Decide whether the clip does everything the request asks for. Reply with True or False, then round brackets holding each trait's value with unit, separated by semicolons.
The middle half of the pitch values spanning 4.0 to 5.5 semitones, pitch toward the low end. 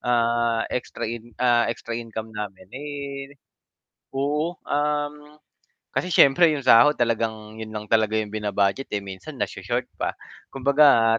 True (4.4 semitones; 120 Hz)